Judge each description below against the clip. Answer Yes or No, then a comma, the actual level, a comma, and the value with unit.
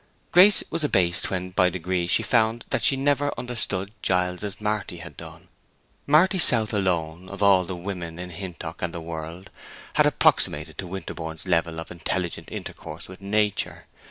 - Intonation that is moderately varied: Yes, average, 3.7 semitones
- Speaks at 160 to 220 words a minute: Yes, average, 170 wpm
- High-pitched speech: No, very low, 95 Hz